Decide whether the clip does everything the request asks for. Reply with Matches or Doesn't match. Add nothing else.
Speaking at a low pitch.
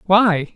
Doesn't match